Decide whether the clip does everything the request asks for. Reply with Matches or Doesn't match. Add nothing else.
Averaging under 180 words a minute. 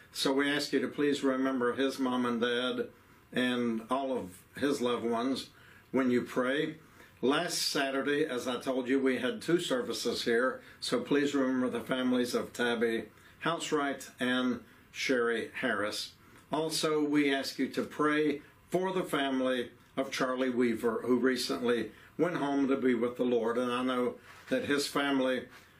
Matches